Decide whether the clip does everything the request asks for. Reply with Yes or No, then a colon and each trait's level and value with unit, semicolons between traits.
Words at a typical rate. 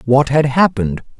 Yes: average, 150 wpm